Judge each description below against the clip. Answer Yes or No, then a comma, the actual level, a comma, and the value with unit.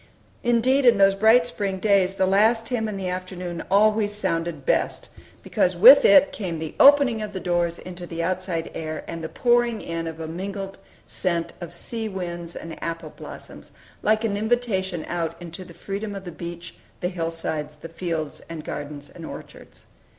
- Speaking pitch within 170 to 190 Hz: Yes, medium, 185 Hz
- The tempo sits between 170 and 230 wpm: Yes, average, 175 wpm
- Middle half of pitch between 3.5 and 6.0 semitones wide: Yes, average, 4.2 semitones